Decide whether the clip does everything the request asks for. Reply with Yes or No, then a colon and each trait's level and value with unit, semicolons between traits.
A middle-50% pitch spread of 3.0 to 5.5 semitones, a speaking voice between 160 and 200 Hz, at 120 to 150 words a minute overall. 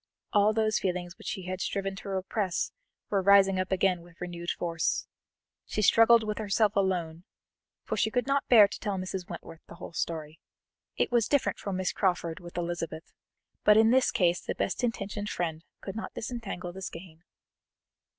No: average, 3.3 semitones; high, 190 Hz; average, 180 wpm